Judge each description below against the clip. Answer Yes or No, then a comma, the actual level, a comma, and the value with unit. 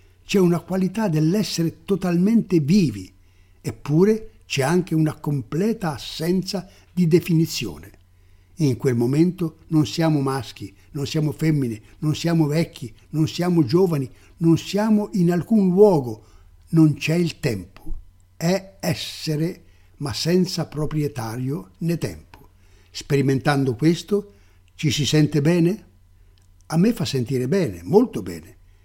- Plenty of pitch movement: Yes, wide, 8.5 semitones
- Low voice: No, medium, 150 Hz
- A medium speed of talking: No, slow, 120 wpm